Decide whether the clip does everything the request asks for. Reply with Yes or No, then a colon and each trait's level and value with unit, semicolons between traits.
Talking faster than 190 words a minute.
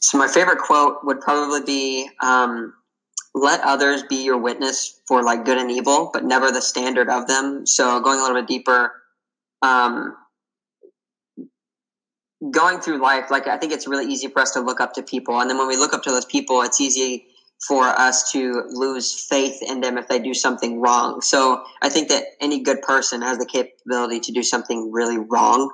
Yes: average, 200 wpm